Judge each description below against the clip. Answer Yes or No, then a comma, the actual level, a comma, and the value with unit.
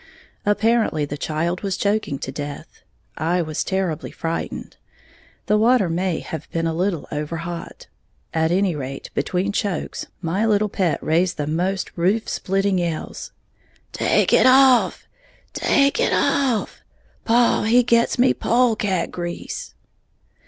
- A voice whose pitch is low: No, medium, 185 Hz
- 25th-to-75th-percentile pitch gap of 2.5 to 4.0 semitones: No, average, 4.7 semitones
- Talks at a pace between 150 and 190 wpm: No, average, 140 wpm